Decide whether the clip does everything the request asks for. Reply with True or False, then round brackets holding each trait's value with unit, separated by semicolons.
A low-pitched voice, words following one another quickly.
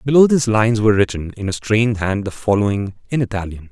True (110 Hz; 210 wpm)